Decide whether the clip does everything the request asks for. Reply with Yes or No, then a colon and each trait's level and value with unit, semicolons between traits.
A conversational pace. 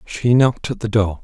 No: fast, 245 wpm